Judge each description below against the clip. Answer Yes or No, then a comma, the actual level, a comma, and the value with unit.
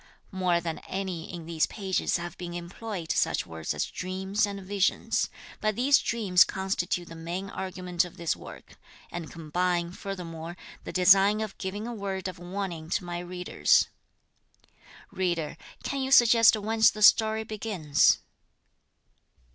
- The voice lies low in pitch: No, medium, 185 Hz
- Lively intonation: No, average, 2.9 semitones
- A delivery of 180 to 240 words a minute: No, average, 145 wpm